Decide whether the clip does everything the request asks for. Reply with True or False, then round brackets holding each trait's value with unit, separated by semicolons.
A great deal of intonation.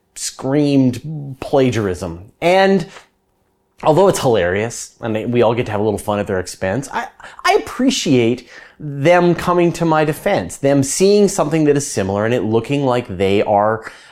True (7.1 semitones)